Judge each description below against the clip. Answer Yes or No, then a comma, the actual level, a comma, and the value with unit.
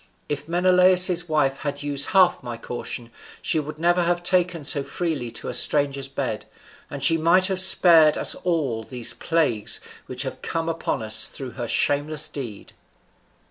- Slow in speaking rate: No, average, 165 wpm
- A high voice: No, medium, 150 Hz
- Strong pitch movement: No, average, 4.3 semitones